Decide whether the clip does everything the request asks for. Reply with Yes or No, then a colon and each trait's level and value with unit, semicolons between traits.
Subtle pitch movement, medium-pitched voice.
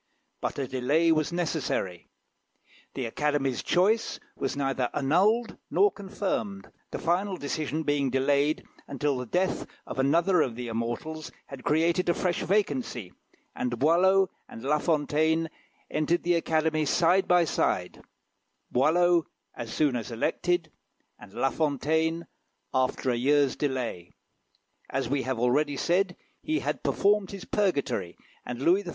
No: average, 4.8 semitones; medium, 150 Hz